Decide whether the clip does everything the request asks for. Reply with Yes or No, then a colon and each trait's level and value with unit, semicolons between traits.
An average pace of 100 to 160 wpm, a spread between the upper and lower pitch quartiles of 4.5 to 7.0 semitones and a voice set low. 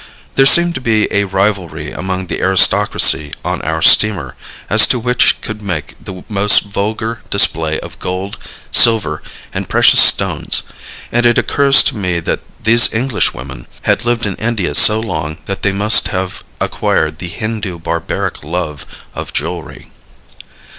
Yes: average, 150 wpm; average, 4.8 semitones; low, 100 Hz